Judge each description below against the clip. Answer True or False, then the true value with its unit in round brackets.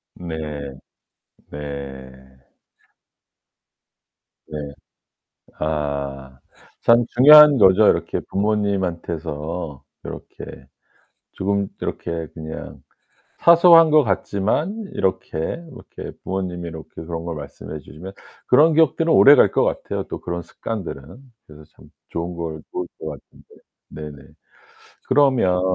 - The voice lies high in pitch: False (85 Hz)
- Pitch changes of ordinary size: False (6.3 semitones)